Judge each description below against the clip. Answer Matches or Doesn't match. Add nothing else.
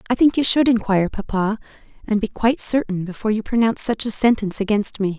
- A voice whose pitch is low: Doesn't match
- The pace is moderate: Doesn't match